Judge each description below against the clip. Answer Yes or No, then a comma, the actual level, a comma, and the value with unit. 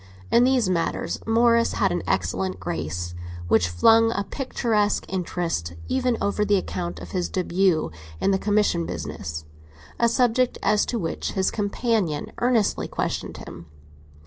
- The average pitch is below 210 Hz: Yes, high, 190 Hz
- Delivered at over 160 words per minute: No, average, 140 wpm